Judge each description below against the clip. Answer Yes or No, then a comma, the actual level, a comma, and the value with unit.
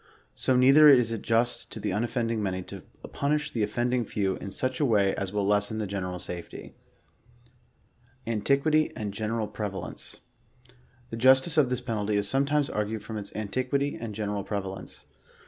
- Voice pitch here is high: No, low, 110 Hz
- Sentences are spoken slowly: No, average, 170 wpm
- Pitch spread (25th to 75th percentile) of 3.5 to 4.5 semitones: Yes, average, 4.0 semitones